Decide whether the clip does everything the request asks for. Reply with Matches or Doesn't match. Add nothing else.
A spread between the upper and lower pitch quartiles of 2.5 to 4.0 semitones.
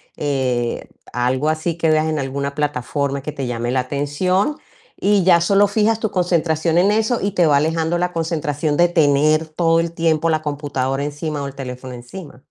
Matches